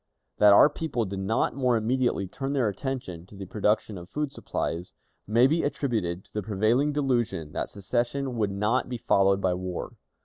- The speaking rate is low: No, average, 180 wpm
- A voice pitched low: Yes, low, 110 Hz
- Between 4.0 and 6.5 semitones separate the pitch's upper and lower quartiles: Yes, average, 5.0 semitones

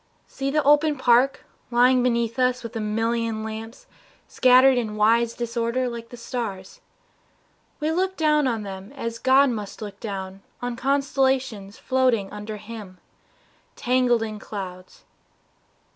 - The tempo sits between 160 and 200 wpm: No, slow, 135 wpm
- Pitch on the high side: Yes, high, 235 Hz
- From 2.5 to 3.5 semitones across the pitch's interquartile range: Yes, average, 3.2 semitones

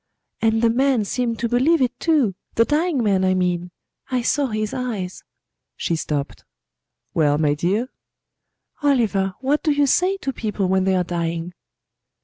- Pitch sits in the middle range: No, high, 225 Hz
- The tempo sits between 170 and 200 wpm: No, average, 160 wpm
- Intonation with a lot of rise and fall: Yes, wide, 6.1 semitones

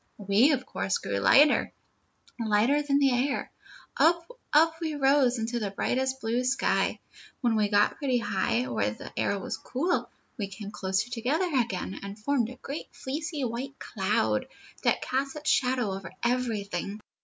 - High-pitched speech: Yes, high, 240 Hz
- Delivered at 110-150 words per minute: No, average, 160 wpm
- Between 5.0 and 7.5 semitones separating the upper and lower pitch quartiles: Yes, average, 5.3 semitones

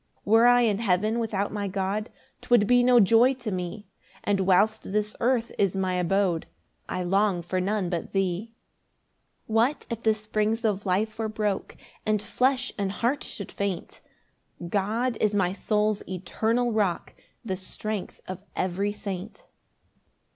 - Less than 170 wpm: Yes, average, 155 wpm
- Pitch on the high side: Yes, high, 210 Hz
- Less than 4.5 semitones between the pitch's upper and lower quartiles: Yes, average, 2.8 semitones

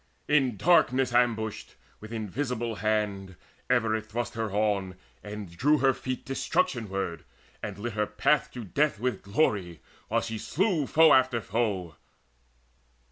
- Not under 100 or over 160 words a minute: Yes, average, 140 wpm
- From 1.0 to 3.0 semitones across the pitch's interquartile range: No, average, 3.9 semitones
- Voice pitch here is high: No, low, 110 Hz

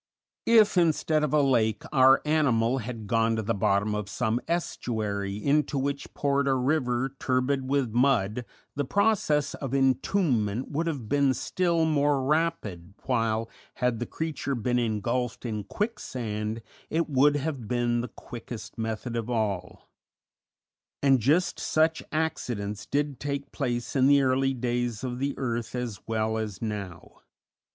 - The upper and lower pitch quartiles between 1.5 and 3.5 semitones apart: No, average, 4.2 semitones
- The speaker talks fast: No, average, 145 wpm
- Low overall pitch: Yes, low, 125 Hz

